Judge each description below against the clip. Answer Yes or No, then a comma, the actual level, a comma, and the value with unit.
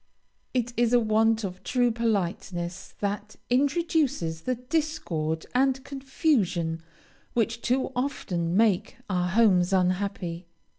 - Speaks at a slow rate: Yes, slow, 110 wpm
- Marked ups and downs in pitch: Yes, wide, 6.0 semitones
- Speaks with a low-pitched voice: No, high, 220 Hz